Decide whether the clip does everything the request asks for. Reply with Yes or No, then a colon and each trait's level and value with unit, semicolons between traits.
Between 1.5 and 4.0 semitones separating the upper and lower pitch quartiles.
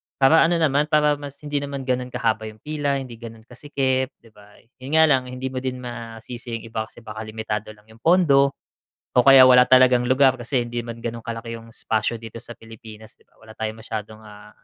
Yes: average, 3.3 semitones